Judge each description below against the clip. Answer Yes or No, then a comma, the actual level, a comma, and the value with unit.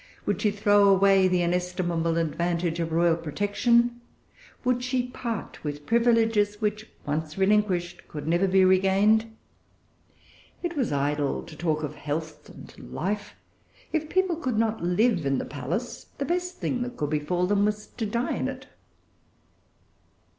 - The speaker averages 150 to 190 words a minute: Yes, average, 155 wpm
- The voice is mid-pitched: No, high, 195 Hz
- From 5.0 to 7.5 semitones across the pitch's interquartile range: Yes, wide, 5.5 semitones